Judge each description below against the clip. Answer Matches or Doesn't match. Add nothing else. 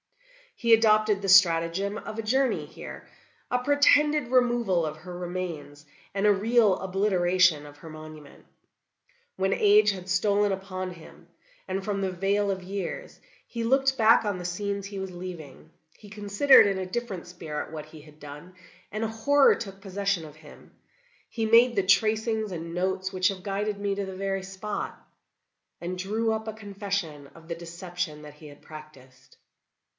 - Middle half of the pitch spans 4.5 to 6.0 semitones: Doesn't match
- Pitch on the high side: Matches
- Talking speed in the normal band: Matches